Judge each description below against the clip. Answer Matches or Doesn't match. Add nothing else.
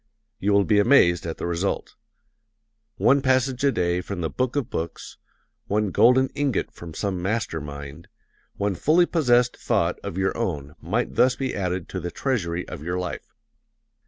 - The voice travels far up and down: Matches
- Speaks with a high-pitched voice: Doesn't match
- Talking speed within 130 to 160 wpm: Doesn't match